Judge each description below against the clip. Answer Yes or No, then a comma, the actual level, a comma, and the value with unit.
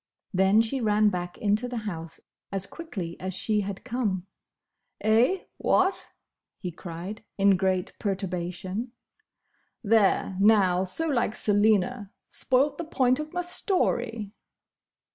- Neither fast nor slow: No, slow, 120 wpm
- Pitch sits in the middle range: No, high, 210 Hz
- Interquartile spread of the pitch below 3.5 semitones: No, average, 4.6 semitones